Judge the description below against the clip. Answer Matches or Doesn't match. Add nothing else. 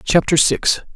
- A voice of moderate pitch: Matches